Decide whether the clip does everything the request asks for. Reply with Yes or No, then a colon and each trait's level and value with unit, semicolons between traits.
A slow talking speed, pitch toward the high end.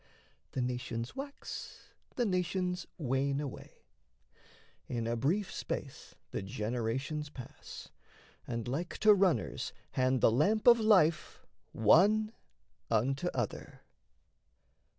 No: slow, 105 wpm; medium, 140 Hz